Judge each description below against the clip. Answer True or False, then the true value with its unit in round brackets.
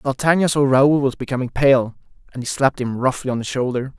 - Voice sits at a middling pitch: False (130 Hz)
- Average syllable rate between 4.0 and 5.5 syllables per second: False (6.0 syllables/s)